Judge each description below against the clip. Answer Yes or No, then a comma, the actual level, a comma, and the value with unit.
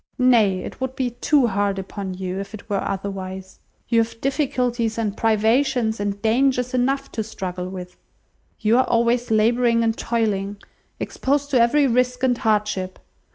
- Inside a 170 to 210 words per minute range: No, average, 155 wpm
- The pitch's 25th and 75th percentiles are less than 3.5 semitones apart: No, average, 3.9 semitones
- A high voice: Yes, high, 225 Hz